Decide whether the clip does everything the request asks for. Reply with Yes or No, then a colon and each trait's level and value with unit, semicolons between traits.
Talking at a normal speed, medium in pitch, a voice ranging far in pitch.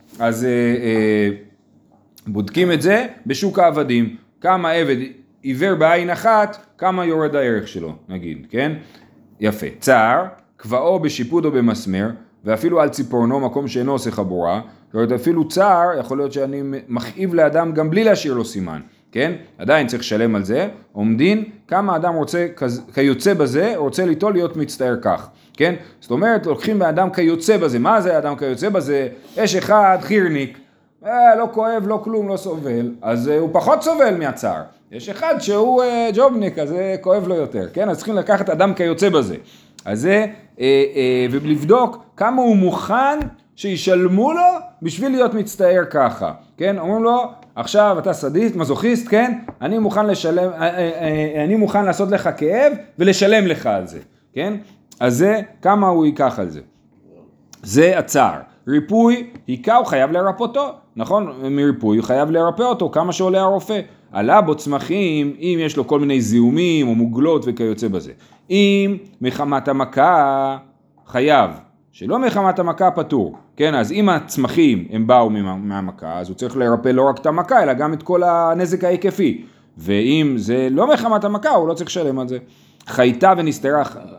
No: fast, 160 wpm; medium, 170 Hz; wide, 7.2 semitones